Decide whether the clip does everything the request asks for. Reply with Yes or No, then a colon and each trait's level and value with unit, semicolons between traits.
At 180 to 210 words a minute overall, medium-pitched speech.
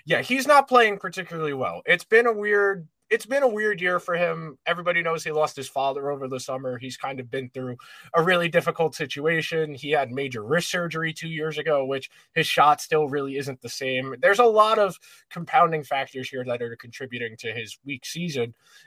Yes: fast, 205 wpm; medium, 155 Hz